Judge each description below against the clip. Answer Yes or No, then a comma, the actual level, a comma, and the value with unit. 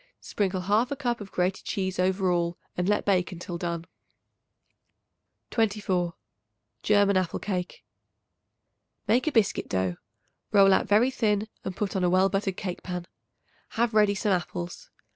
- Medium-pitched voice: No, high, 195 Hz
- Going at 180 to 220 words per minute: No, average, 145 wpm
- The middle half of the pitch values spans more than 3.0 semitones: No, average, 2.7 semitones